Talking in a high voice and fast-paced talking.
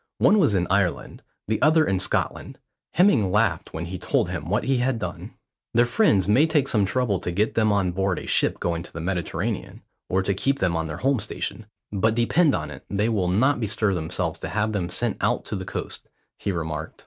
No: low, 100 Hz; fast, 220 wpm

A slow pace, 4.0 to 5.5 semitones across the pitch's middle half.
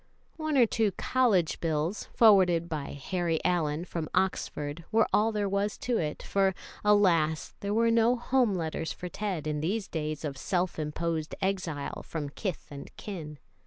No: average, 165 wpm; average, 4.9 semitones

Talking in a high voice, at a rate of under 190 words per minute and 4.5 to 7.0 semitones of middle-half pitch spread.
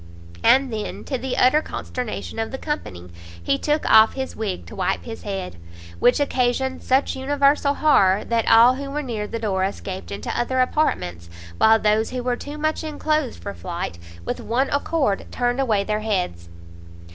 Yes: high, 240 Hz; average, 175 wpm; average, 5.2 semitones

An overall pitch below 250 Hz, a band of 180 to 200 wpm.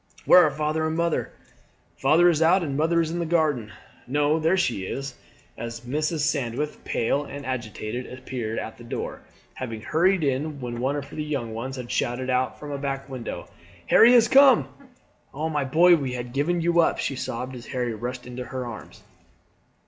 Yes: medium, 140 Hz; average, 190 wpm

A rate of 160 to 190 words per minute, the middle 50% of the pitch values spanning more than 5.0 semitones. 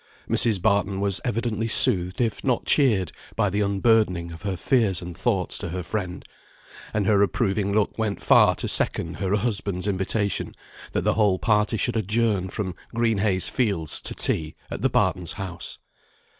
No: average, 170 wpm; average, 3.1 semitones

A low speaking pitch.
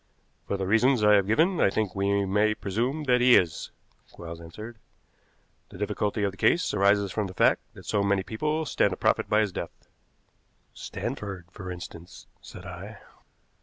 Yes: low, 100 Hz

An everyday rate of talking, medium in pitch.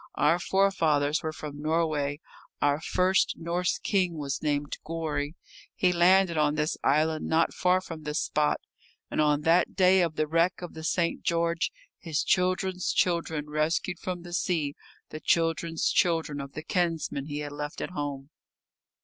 Yes: average, 160 wpm; medium, 160 Hz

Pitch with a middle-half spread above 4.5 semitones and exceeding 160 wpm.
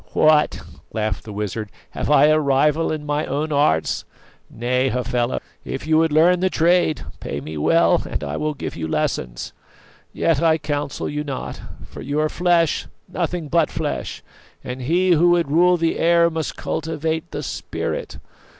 No: average, 3.8 semitones; average, 170 wpm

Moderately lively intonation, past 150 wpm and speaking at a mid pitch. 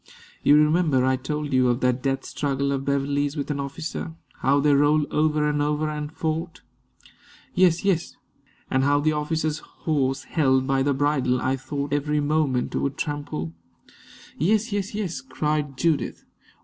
No: narrow, 2.3 semitones; average, 165 wpm; medium, 145 Hz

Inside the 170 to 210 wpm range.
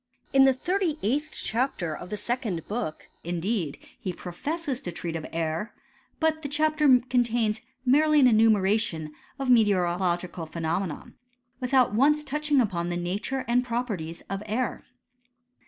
No: average, 140 wpm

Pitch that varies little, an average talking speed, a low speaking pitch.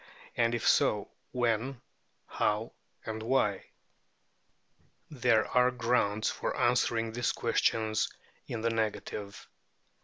No: narrow, 2.0 semitones; slow, 100 wpm; low, 115 Hz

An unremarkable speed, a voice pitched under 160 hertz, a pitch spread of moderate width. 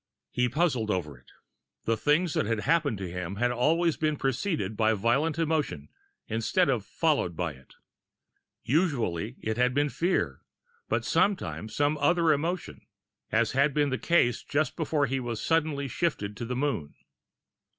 No: average, 160 wpm; low, 135 Hz; wide, 6.1 semitones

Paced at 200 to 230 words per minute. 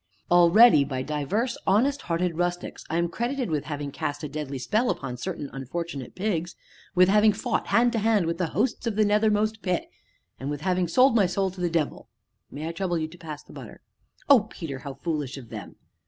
Yes: fast, 205 wpm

